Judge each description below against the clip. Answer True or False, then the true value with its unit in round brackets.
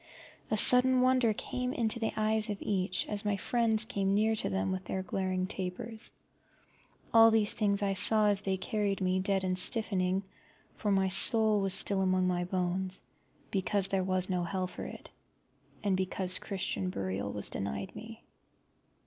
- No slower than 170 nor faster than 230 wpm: True (175 wpm)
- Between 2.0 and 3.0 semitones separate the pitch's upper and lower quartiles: True (2.7 semitones)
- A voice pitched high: True (195 Hz)